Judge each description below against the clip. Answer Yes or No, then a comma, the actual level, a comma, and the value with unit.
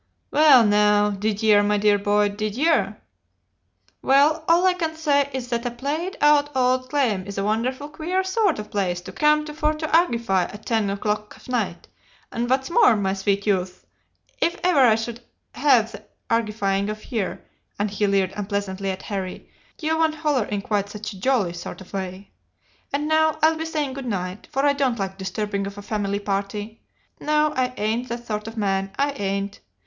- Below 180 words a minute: No, average, 195 wpm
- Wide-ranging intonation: Yes, wide, 6.1 semitones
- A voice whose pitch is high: Yes, high, 220 Hz